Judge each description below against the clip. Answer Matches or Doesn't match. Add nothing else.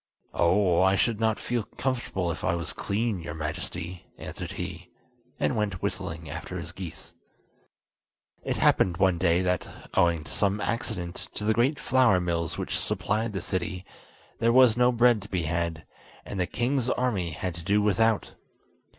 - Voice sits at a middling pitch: Doesn't match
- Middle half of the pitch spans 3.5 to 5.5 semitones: Matches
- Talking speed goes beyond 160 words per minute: Matches